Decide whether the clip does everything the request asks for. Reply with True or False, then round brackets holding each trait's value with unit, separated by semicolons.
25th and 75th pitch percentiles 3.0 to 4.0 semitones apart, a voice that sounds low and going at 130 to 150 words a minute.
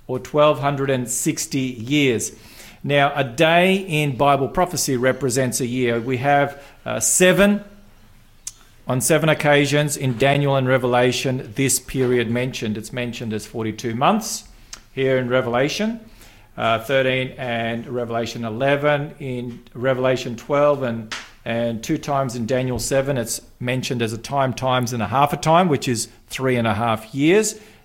True (3.3 semitones; 130 Hz; 145 wpm)